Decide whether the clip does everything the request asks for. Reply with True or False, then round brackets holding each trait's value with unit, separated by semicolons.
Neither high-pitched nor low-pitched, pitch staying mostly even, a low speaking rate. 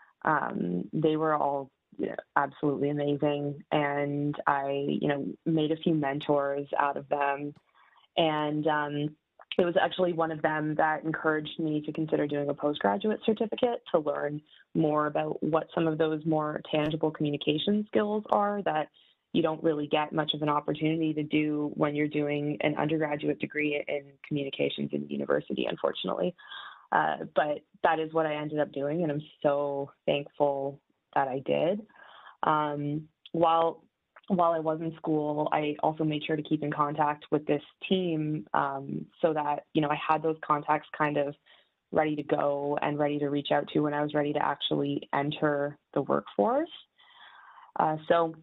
False (150 Hz; 1.6 semitones; 170 wpm)